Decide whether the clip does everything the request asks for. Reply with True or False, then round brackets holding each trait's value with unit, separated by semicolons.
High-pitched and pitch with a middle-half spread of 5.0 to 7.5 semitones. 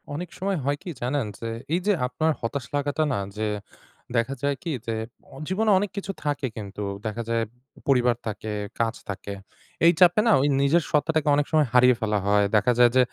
False (135 Hz; 5.5 semitones)